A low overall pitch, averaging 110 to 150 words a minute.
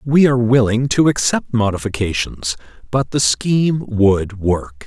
Yes: low, 115 Hz; slow, 135 wpm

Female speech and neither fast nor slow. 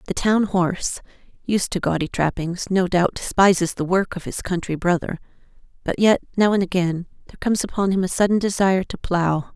Yes: female; average, 190 wpm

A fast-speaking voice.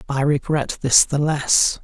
No: average, 165 wpm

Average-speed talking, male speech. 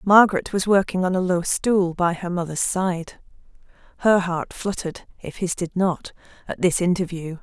No: average, 170 wpm; female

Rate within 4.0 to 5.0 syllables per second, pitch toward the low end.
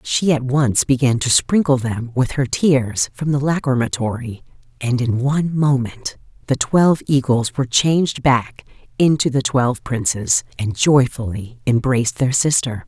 Yes: 4.5 syllables/s; low, 130 Hz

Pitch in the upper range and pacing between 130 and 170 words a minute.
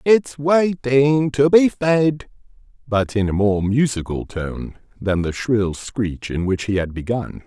No: low, 120 Hz; average, 160 wpm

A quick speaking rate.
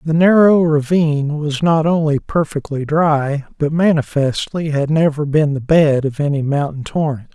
No: average, 155 wpm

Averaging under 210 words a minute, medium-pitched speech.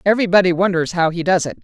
No: fast, 220 wpm; medium, 180 Hz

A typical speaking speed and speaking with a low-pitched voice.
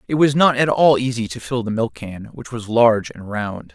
No: fast, 255 wpm; low, 120 Hz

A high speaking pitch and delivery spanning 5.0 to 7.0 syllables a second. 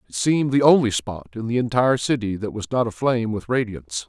No: low, 115 Hz; 6.4 syllables/s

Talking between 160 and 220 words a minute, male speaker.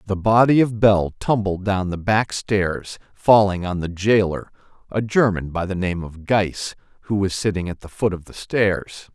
Yes: average, 190 wpm; male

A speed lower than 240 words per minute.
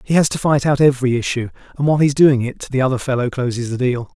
No: fast, 275 wpm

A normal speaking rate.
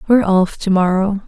Yes: average, 190 wpm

